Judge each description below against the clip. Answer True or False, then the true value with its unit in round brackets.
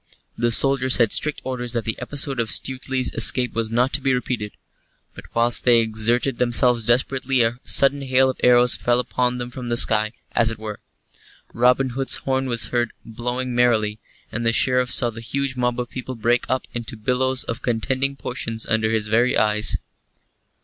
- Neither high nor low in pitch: False (120 Hz)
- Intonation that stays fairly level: True (2.1 semitones)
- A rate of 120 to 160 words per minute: False (185 wpm)